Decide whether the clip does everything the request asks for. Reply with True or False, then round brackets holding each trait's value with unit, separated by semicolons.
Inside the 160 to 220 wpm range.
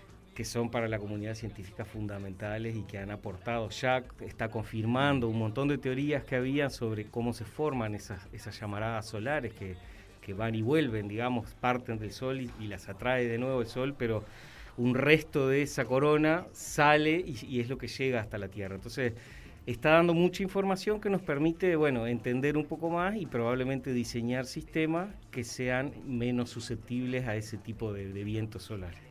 True (185 wpm)